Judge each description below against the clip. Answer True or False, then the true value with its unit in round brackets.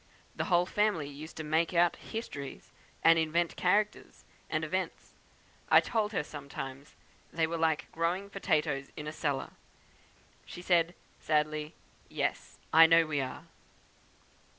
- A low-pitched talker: False (160 Hz)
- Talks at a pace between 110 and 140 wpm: True (135 wpm)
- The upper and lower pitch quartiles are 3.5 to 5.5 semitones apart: False (2.6 semitones)